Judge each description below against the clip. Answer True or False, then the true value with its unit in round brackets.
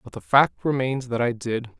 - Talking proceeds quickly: True (235 wpm)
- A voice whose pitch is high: False (125 Hz)